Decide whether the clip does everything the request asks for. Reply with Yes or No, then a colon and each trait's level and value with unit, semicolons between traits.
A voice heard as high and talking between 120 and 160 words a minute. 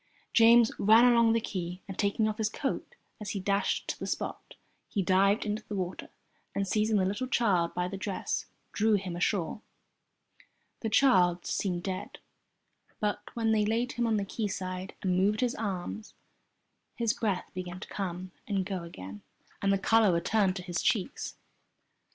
No: high, 200 Hz; average, 170 wpm